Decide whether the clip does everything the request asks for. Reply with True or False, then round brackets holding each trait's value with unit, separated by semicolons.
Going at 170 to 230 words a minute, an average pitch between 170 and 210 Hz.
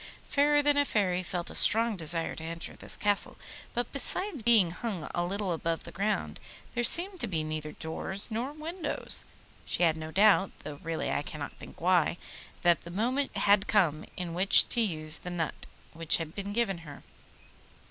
True (185 wpm; 190 Hz)